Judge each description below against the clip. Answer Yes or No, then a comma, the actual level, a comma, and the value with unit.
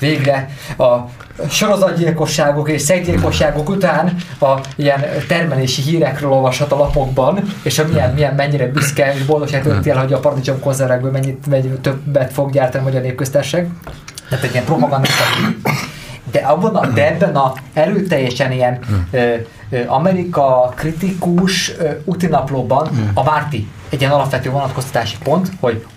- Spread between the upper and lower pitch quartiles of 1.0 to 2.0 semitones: No, average, 2.8 semitones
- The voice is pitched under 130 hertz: No, medium, 140 Hz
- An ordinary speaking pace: Yes, average, 125 wpm